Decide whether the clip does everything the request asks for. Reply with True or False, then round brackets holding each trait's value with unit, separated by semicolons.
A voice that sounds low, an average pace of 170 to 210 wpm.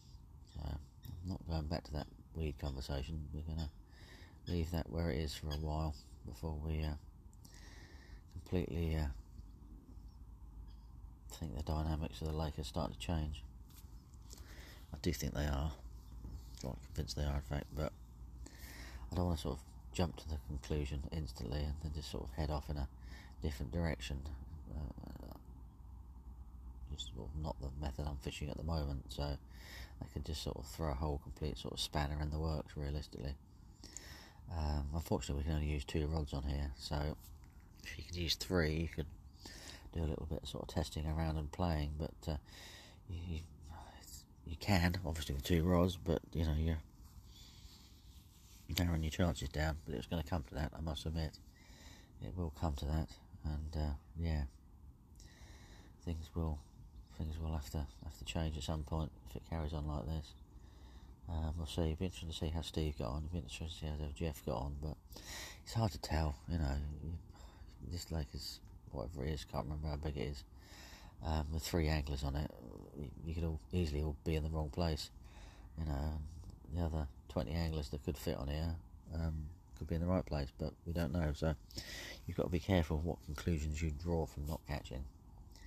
True (80 Hz; 190 wpm)